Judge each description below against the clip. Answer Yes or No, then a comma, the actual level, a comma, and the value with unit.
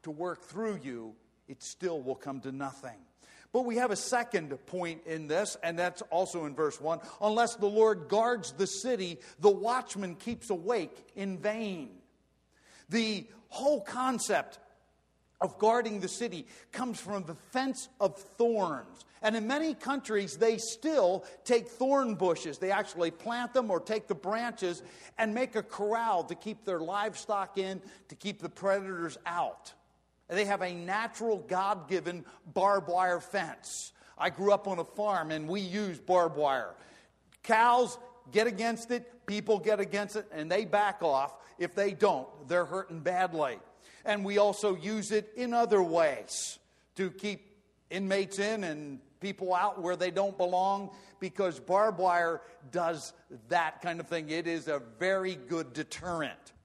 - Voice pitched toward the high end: Yes, high, 195 Hz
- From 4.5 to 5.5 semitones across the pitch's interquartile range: No, average, 3.9 semitones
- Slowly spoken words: No, average, 160 wpm